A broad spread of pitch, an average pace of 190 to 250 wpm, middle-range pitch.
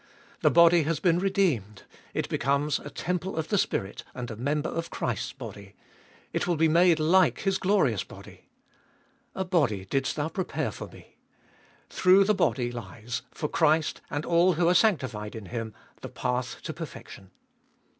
No: wide, 6.4 semitones; average, 165 wpm; medium, 150 Hz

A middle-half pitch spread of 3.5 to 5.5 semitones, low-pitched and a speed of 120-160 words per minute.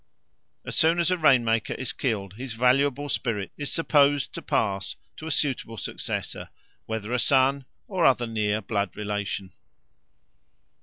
Yes: average, 5.1 semitones; low, 125 Hz; average, 150 wpm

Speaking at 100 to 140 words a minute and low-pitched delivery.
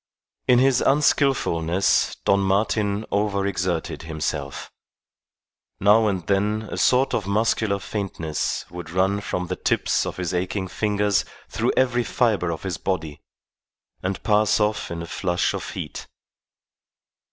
Yes: slow, 135 wpm; low, 100 Hz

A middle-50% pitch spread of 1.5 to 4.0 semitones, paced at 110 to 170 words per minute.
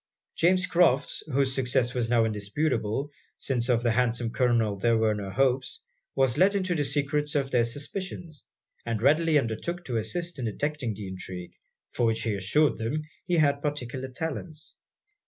No: average, 4.6 semitones; average, 165 wpm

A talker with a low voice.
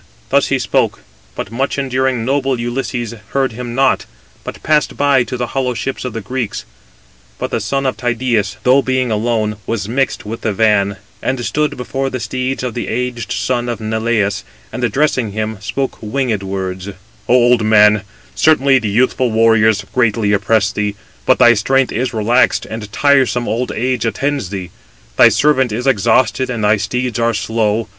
Yes: low, 120 Hz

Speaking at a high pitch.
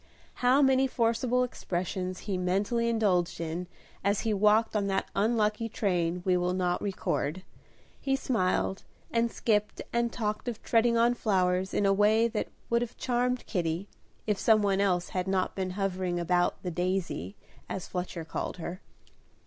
Yes: high, 200 Hz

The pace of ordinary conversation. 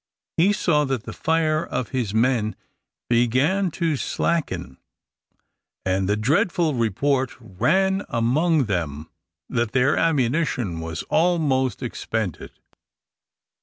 No: slow, 110 wpm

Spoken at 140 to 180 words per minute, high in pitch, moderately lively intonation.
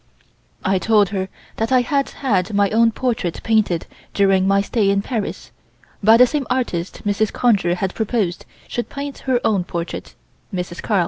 Yes: average, 170 wpm; high, 205 Hz; average, 3.9 semitones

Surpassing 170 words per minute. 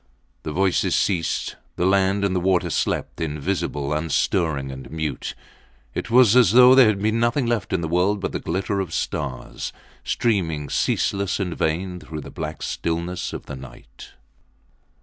No: average, 165 wpm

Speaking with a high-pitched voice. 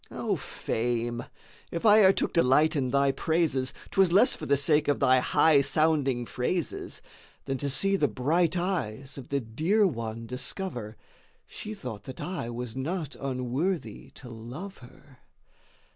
No: medium, 140 Hz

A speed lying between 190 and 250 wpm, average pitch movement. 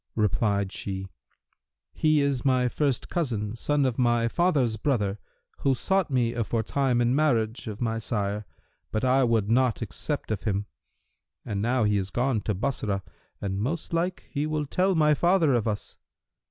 No: average, 165 wpm; average, 5.0 semitones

